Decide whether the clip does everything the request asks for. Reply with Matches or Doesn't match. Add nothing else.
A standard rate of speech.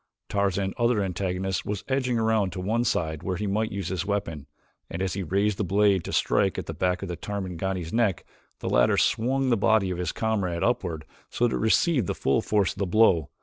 Doesn't match